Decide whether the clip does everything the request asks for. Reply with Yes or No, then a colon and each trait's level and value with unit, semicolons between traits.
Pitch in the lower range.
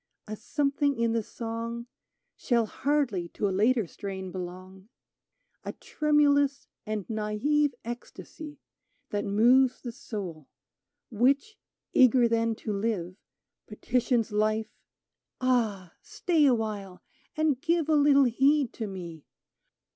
No: high, 230 Hz